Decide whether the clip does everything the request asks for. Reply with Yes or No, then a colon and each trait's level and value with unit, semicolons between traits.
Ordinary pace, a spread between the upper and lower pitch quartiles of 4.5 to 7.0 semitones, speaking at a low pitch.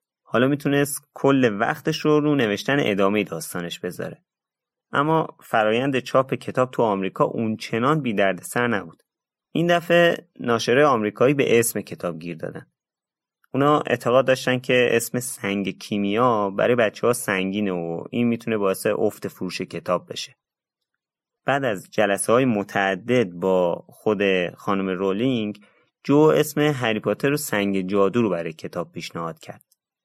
Yes: average, 140 wpm; average, 5.2 semitones; low, 110 Hz